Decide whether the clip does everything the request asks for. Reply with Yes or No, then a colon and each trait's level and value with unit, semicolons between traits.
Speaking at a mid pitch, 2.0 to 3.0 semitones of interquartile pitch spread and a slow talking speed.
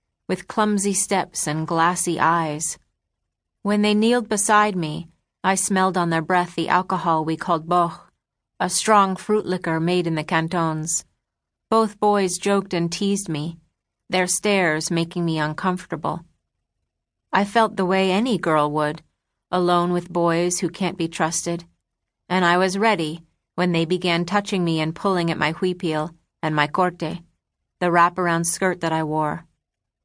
No: medium, 175 Hz; average, 2.7 semitones; average, 155 wpm